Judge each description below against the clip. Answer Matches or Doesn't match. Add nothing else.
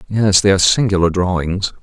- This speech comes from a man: Matches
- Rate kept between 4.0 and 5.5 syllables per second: Doesn't match